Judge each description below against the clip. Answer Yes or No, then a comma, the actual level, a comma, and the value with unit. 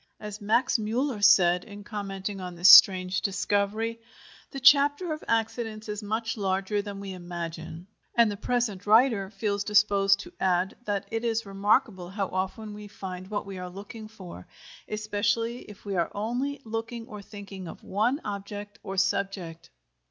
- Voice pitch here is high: Yes, high, 205 Hz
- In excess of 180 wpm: No, average, 160 wpm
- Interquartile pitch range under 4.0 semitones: Yes, narrow, 2.6 semitones